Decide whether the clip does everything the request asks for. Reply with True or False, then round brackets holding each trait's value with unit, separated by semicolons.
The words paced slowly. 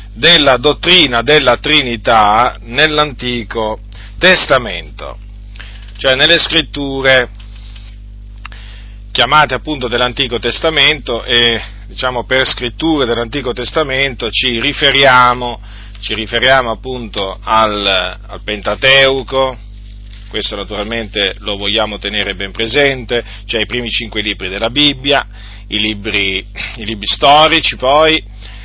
True (100 wpm)